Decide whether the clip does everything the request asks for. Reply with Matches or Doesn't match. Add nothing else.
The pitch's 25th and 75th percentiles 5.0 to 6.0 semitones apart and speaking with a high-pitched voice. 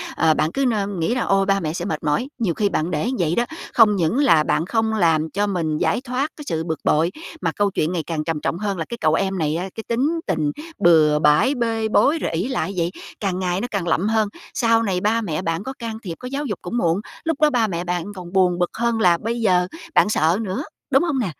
Matches